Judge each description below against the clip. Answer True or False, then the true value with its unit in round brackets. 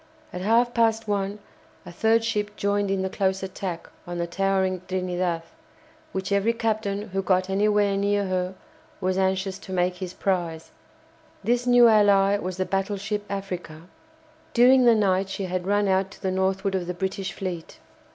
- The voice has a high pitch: True (195 Hz)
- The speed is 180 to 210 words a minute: False (170 wpm)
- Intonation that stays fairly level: True (1.8 semitones)